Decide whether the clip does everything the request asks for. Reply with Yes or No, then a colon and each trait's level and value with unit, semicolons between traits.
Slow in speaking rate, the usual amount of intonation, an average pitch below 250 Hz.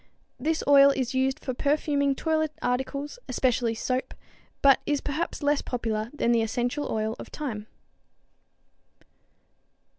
No: slow, 125 wpm; average, 3.2 semitones; very high, 265 Hz